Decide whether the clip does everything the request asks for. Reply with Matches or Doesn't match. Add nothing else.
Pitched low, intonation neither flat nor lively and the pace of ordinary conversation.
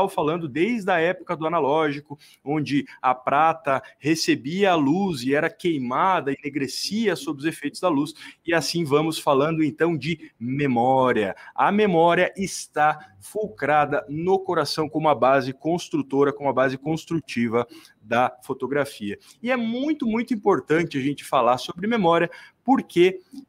Doesn't match